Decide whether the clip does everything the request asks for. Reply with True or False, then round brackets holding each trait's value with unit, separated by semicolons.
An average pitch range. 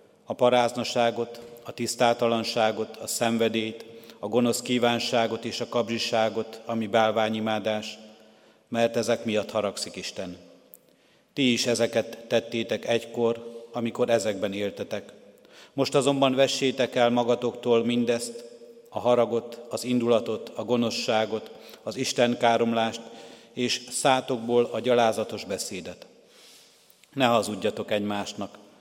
False (1.3 semitones)